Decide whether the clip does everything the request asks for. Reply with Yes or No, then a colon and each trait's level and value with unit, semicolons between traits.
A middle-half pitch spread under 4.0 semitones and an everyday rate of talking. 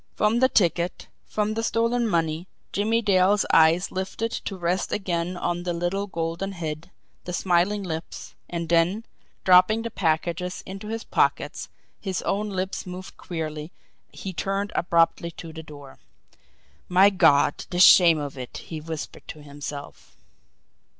Yes: average, 3.2 semitones; average, 145 wpm